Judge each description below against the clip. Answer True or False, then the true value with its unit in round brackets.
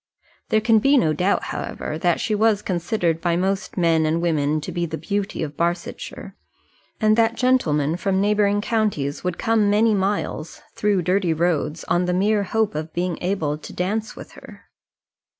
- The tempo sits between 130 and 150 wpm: False (175 wpm)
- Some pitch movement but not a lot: True (4.2 semitones)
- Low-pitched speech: False (185 Hz)